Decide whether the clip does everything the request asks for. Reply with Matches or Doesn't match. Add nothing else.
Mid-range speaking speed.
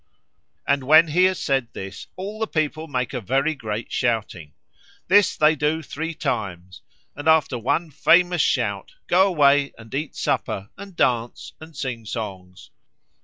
Matches